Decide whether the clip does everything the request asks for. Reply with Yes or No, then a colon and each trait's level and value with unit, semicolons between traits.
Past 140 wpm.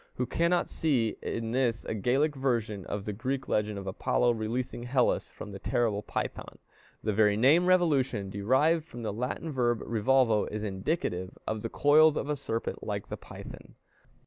Yes: average, 170 wpm